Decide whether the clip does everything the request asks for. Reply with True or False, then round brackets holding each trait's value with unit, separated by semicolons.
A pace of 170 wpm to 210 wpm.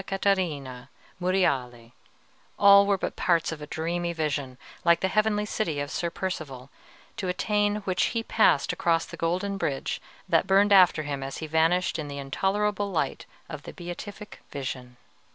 False (160 wpm)